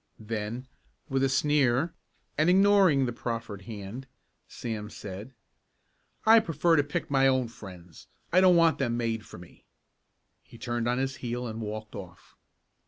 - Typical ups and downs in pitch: Yes, average, 4.8 semitones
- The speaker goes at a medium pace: Yes, average, 155 wpm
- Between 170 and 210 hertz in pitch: No, low, 120 Hz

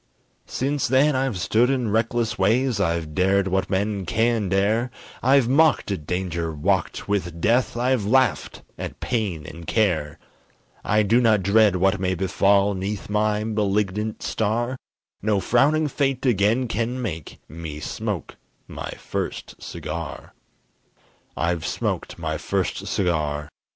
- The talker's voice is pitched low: Yes, low, 105 Hz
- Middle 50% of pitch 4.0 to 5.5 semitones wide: Yes, average, 4.3 semitones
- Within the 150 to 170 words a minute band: No, slow, 135 wpm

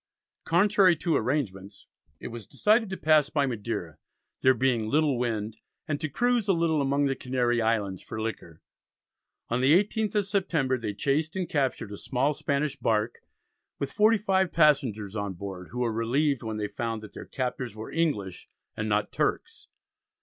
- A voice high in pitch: No, low, 130 Hz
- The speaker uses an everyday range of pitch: No, wide, 6.4 semitones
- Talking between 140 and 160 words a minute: No, average, 170 wpm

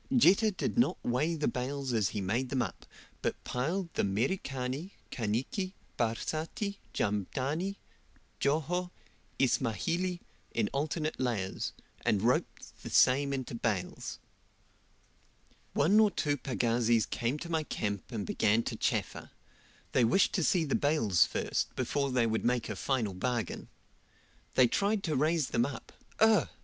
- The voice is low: Yes, low, 130 Hz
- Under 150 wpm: Yes, average, 140 wpm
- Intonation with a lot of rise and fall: Yes, wide, 5.8 semitones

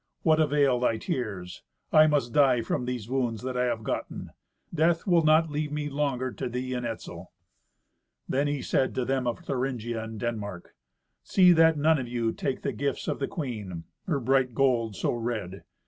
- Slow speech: No, average, 180 wpm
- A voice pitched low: Yes, low, 130 Hz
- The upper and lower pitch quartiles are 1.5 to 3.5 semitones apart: No, average, 3.9 semitones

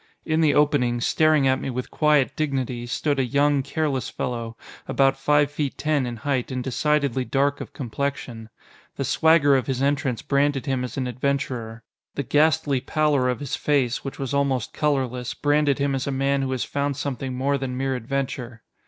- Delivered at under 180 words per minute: No, average, 185 wpm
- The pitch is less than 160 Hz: Yes, low, 135 Hz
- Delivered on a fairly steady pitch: Yes, narrow, 2.1 semitones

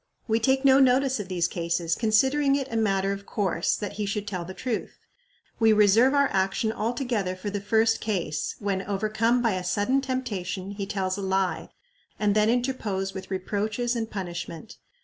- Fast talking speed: No, average, 180 wpm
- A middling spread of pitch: Yes, average, 3.7 semitones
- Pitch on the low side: No, high, 210 Hz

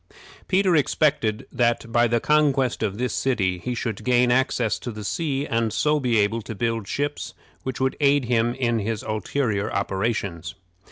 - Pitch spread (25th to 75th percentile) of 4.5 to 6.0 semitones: No, average, 3.5 semitones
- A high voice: No, low, 120 Hz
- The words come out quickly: No, average, 170 wpm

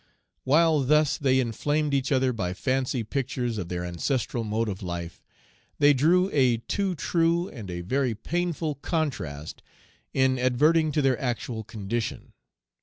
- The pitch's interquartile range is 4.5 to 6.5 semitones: Yes, average, 5.2 semitones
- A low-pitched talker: Yes, low, 130 Hz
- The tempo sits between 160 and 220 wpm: No, average, 145 wpm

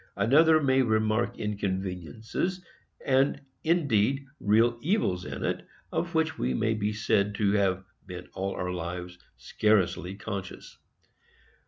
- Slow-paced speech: Yes, slow, 125 wpm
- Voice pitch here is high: No, low, 105 Hz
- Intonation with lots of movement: Yes, wide, 5.7 semitones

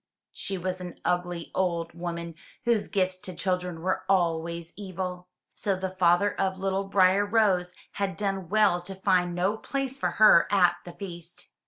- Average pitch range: No, narrow, 1.9 semitones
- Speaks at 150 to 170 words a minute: Yes, average, 165 wpm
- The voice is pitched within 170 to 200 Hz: Yes, medium, 185 Hz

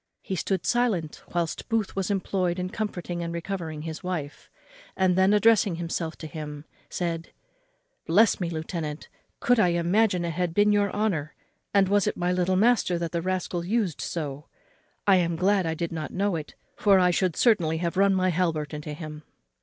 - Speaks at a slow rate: No, average, 185 wpm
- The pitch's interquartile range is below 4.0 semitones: Yes, average, 3.0 semitones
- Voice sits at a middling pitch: Yes, medium, 180 Hz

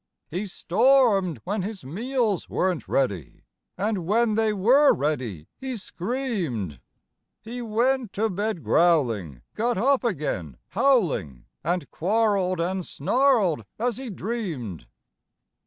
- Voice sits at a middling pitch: No, high, 195 Hz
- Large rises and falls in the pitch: Yes, wide, 7.1 semitones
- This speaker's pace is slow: Yes, slow, 115 wpm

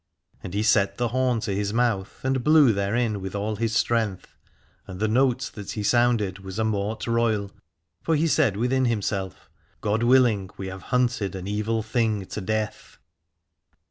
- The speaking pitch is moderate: No, low, 110 Hz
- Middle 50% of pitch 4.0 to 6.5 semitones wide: No, average, 3.2 semitones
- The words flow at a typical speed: Yes, average, 175 wpm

